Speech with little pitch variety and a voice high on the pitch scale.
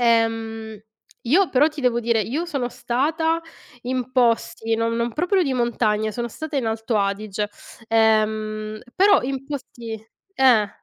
No: average, 3.4 semitones; high, 235 Hz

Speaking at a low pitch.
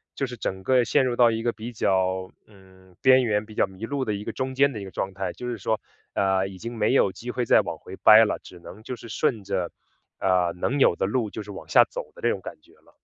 Yes: low, 105 Hz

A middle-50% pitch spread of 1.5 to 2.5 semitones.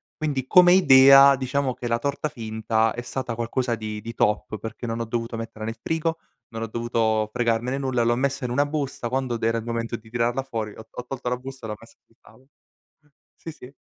No: average, 2.9 semitones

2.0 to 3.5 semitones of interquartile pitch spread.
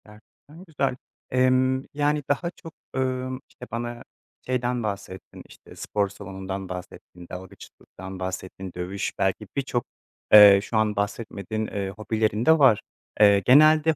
No: average, 4.7 semitones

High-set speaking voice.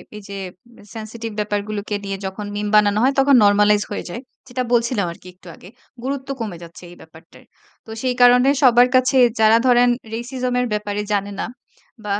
Yes: high, 215 Hz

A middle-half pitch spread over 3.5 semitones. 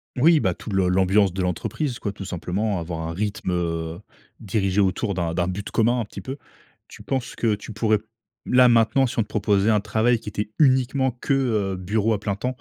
Yes: average, 4.0 semitones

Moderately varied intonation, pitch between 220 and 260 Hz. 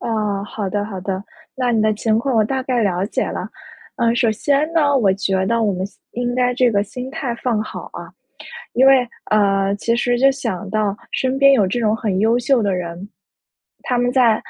Yes: average, 3.7 semitones; high, 225 Hz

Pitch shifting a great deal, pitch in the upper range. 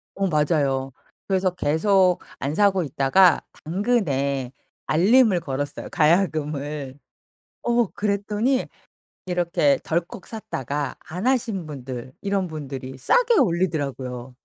No: wide, 6.0 semitones; medium, 165 Hz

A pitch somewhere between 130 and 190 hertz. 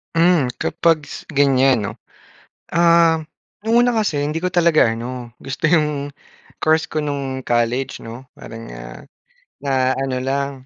Yes: medium, 140 Hz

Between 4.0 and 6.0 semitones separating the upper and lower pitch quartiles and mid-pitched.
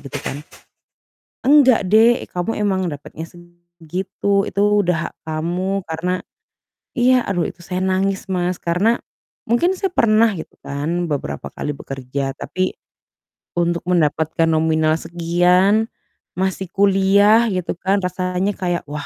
No: average, 3.3 semitones; medium, 180 Hz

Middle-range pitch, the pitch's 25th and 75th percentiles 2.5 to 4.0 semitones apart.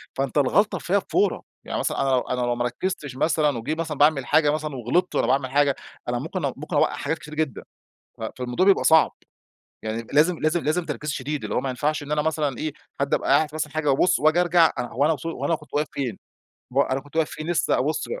Yes: medium, 150 Hz; average, 2.9 semitones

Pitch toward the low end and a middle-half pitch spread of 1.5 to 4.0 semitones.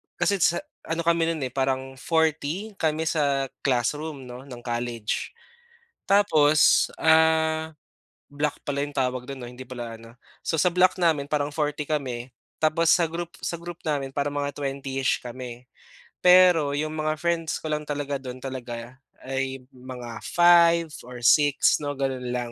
No: medium, 145 Hz; average, 3.7 semitones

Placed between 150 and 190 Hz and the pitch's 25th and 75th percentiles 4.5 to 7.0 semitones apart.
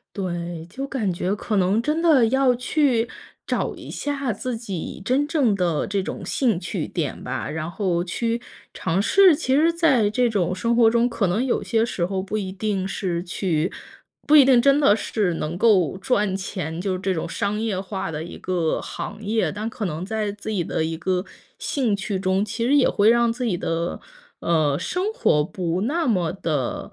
No: high, 205 Hz; average, 5.1 semitones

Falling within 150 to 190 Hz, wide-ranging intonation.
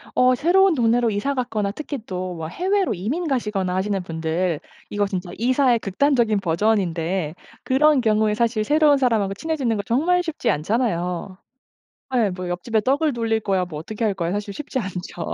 No: high, 215 Hz; wide, 5.8 semitones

